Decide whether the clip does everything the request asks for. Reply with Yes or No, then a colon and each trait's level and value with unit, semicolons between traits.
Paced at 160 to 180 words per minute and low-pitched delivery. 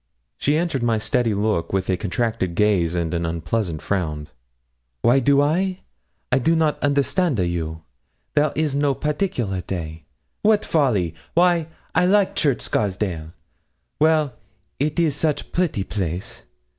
No: average, 145 wpm; low, 120 Hz